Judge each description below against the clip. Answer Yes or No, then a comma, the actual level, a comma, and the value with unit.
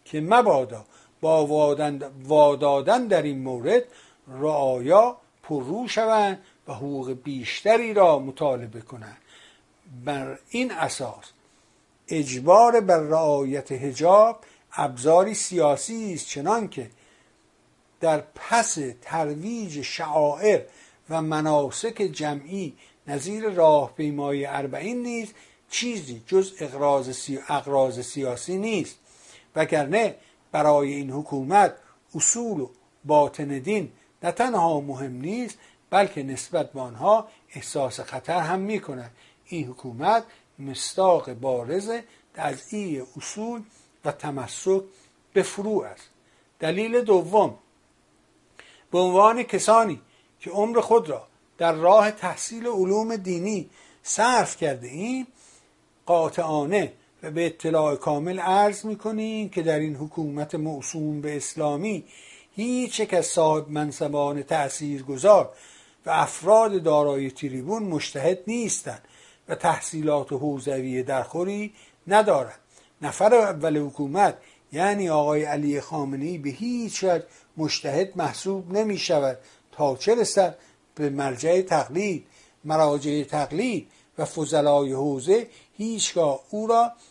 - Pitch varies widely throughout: Yes, wide, 6.3 semitones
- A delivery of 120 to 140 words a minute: No, slow, 105 wpm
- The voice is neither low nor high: Yes, medium, 160 Hz